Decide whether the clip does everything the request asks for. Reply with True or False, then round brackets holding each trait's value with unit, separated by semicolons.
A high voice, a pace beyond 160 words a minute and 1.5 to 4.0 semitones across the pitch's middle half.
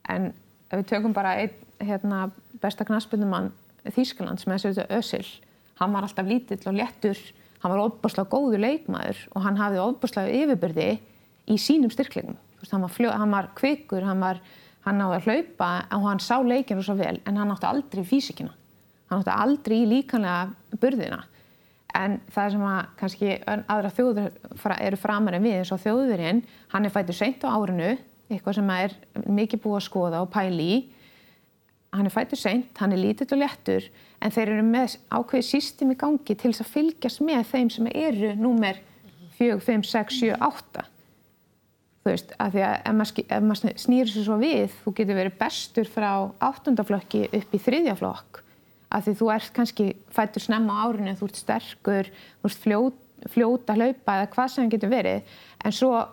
True (215 Hz; 180 wpm; 3.5 semitones)